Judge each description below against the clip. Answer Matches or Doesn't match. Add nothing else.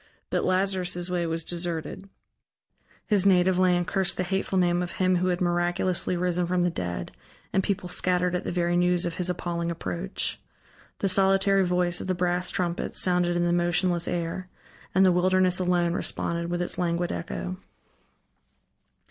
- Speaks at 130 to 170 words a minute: Matches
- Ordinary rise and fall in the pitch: Doesn't match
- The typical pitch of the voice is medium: Matches